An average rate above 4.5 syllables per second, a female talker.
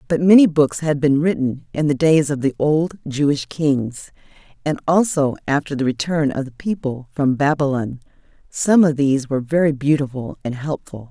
Yes: 5.0 syllables/s; female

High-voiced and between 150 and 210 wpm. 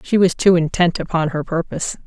No: medium, 170 Hz; fast, 205 wpm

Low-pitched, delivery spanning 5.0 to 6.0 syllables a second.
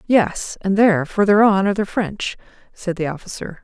No: high, 195 Hz; 5.2 syllables/s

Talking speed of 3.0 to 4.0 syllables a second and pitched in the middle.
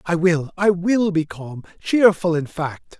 Yes: 3.8 syllables/s; medium, 175 Hz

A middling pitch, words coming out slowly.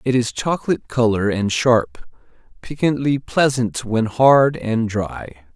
No: low, 120 Hz; slow, 130 wpm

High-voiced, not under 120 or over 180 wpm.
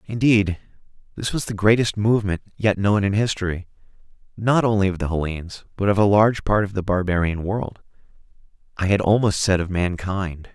No: low, 100 Hz; average, 165 wpm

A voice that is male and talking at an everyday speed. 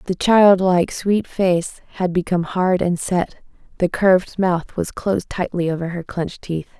No: female; average, 170 wpm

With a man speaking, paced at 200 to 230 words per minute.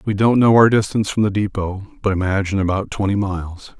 Yes: male; fast, 205 wpm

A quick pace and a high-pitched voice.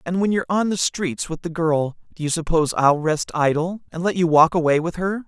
No: fast, 250 wpm; medium, 170 Hz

